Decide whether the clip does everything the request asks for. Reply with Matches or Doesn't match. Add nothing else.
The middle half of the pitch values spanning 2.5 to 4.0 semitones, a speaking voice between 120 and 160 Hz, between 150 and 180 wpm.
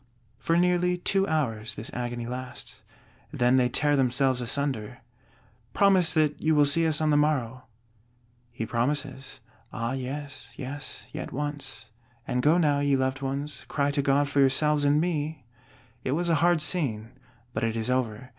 Matches